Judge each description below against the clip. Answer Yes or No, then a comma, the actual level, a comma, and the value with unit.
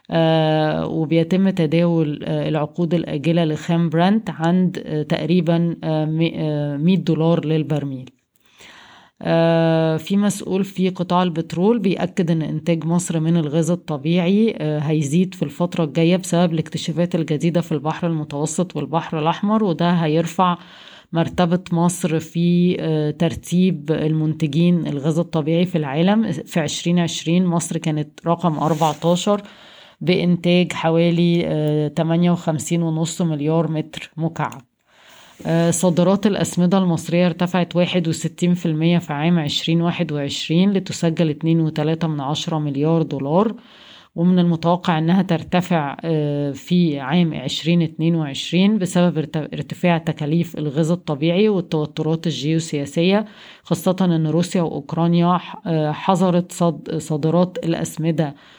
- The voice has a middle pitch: Yes, medium, 165 Hz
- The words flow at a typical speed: Yes, average, 100 wpm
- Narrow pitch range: Yes, narrow, 2.0 semitones